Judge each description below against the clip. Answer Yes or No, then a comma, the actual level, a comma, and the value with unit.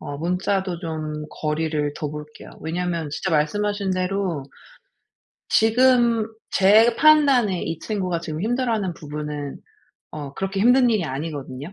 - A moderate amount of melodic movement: No, wide, 5.7 semitones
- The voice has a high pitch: No, medium, 180 Hz